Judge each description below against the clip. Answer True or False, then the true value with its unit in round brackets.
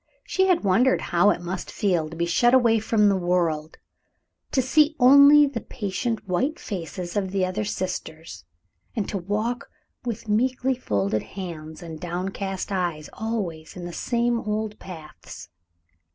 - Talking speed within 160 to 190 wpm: False (150 wpm)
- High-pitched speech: True (195 Hz)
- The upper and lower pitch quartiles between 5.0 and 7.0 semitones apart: True (5.3 semitones)